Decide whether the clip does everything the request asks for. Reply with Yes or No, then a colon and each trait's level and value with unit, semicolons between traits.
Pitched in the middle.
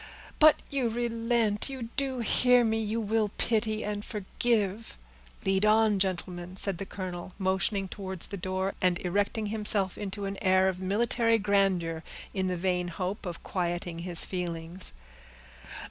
No: high, 195 Hz